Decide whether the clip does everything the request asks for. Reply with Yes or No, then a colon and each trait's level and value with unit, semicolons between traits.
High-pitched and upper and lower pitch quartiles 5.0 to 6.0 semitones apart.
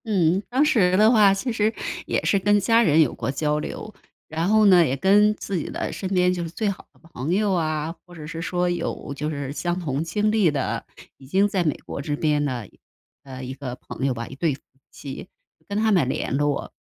No: medium, 175 Hz; wide, 5.6 semitones